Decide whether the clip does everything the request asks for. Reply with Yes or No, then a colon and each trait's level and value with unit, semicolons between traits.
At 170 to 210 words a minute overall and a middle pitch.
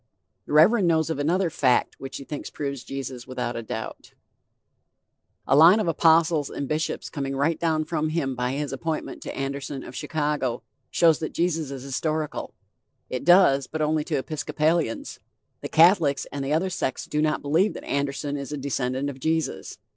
Yes: average, 175 wpm; medium, 150 Hz